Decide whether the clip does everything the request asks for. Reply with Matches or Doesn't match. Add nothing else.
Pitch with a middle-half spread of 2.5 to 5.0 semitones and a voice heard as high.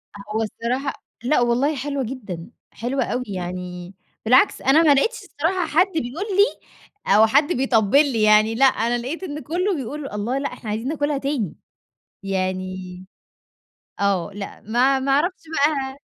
Doesn't match